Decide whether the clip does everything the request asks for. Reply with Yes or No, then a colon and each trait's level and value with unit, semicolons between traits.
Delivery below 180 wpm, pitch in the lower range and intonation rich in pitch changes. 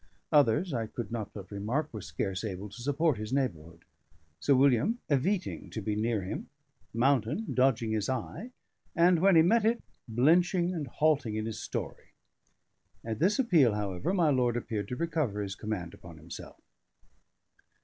Yes: average, 160 wpm; low, 120 Hz; wide, 7.1 semitones